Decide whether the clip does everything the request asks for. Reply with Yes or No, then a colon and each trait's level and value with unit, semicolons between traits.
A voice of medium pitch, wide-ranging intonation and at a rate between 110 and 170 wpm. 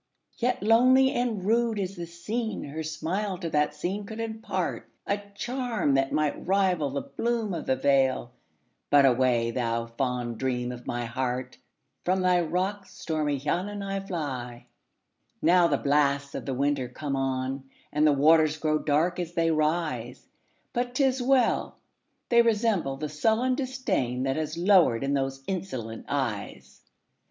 Yes: medium, 155 Hz; wide, 7.0 semitones; slow, 135 wpm